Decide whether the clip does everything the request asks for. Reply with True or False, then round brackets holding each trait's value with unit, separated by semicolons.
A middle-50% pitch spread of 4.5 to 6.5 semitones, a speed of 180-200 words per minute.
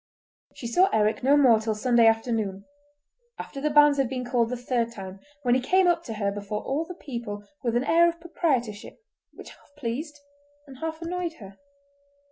True (5.2 semitones; 190 wpm)